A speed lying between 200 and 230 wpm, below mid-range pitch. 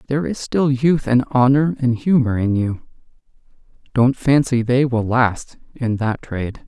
No: average, 160 wpm; low, 125 Hz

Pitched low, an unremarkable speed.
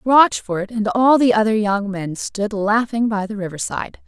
No: high, 215 Hz; average, 190 wpm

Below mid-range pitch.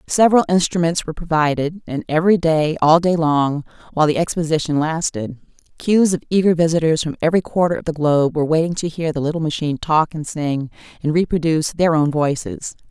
No: medium, 160 Hz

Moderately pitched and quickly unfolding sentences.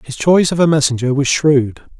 Yes: medium, 145 Hz; fast, 210 wpm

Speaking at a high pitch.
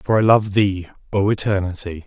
No: low, 100 Hz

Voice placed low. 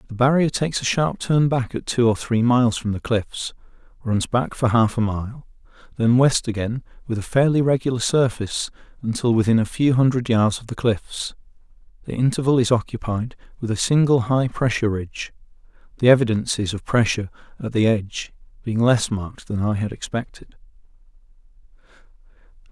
Yes: low, 120 Hz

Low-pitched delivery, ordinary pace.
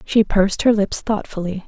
No: high, 200 Hz; average, 180 wpm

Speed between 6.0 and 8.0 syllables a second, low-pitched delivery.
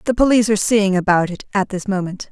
No: 6.7 syllables/s; high, 200 Hz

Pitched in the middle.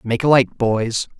No: low, 120 Hz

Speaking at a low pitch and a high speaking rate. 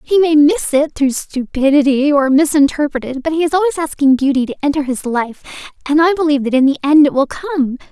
No: very high, 290 Hz; fast, 220 wpm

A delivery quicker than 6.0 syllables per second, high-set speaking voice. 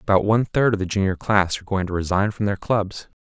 No: 6.2 syllables/s; low, 100 Hz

